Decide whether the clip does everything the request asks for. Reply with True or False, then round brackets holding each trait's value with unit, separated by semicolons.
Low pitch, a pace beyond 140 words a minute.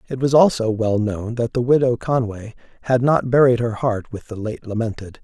True (120 Hz; 205 wpm)